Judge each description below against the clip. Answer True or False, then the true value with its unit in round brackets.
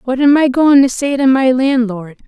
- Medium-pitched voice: False (260 Hz)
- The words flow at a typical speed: False (240 wpm)